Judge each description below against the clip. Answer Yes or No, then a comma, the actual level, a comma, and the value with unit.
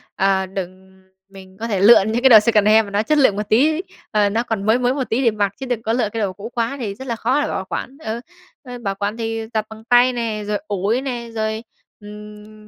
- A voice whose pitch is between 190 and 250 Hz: Yes, high, 220 Hz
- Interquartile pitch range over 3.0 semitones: No, average, 2.7 semitones